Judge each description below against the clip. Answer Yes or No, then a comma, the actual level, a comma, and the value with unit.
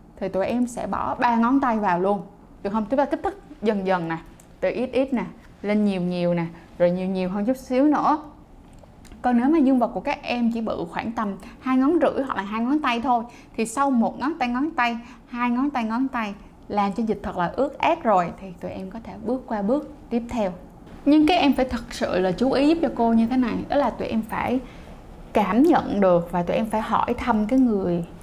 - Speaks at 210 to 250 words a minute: Yes, average, 245 wpm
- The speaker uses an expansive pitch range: No, average, 4.4 semitones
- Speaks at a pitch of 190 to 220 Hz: No, high, 235 Hz